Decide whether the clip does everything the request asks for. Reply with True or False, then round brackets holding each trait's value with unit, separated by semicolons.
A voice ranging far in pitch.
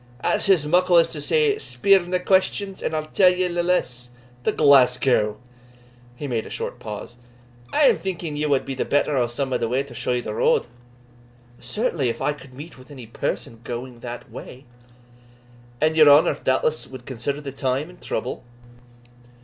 True (5.7 semitones)